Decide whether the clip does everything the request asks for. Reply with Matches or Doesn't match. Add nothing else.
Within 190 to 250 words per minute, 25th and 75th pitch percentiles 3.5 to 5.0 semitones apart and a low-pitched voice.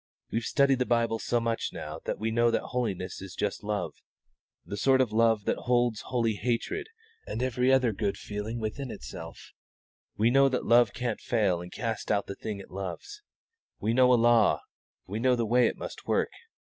Doesn't match